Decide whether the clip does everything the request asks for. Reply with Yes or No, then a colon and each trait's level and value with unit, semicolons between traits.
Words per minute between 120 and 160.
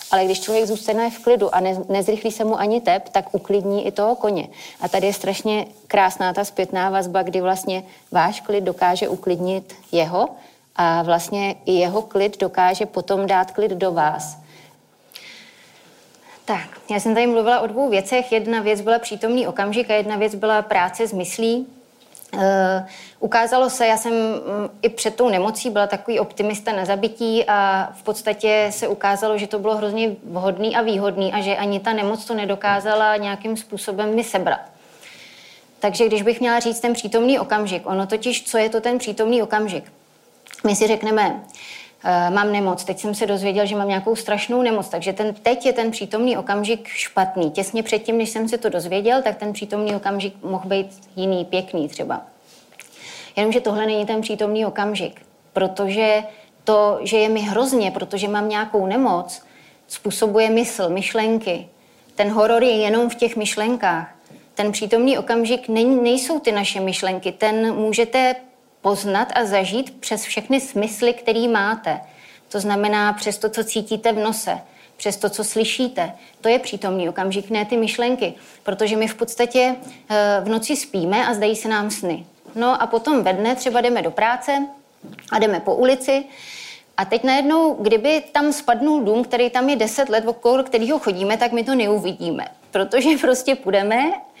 No: fast, 170 wpm